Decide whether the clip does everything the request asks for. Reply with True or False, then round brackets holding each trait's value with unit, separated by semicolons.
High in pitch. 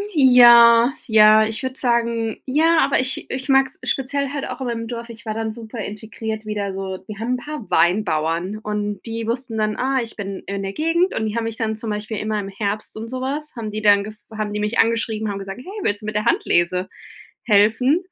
True (220 Hz)